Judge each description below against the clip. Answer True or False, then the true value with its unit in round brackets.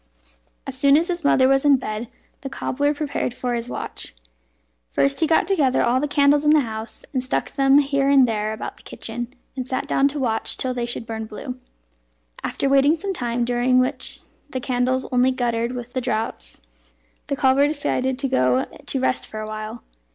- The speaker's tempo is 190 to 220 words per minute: True (195 wpm)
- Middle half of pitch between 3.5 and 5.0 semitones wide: False (2.8 semitones)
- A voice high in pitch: True (255 Hz)